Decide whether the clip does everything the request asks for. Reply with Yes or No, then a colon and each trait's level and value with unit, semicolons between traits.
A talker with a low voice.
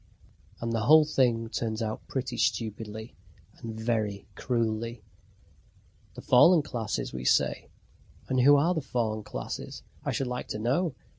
Yes: low, 115 Hz